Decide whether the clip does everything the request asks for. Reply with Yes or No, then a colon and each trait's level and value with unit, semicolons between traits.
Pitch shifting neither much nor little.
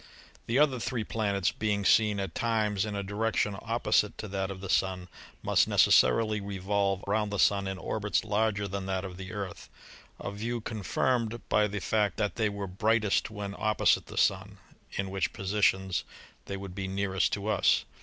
No: narrow, 1.9 semitones